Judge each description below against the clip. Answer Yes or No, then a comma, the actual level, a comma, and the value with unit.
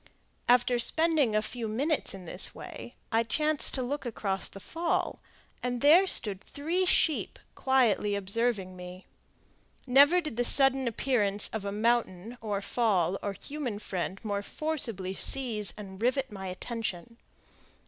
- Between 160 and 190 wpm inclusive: No, average, 145 wpm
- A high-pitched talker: Yes, high, 230 Hz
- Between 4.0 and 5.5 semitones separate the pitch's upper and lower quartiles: Yes, average, 5.2 semitones